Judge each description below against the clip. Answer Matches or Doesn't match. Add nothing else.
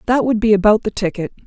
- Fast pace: Matches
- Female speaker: Matches